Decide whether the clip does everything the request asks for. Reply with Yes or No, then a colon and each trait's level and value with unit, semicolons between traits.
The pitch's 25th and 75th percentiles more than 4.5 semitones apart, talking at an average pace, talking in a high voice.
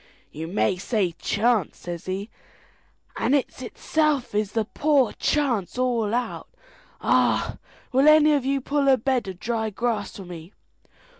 Yes: wide, 5.5 semitones; average, 150 wpm; high, 235 Hz